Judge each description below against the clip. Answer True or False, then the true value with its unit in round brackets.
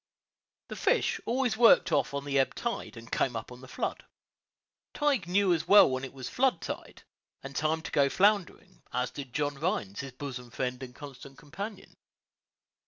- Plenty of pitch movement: True (7.0 semitones)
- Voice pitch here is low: False (145 Hz)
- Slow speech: False (180 wpm)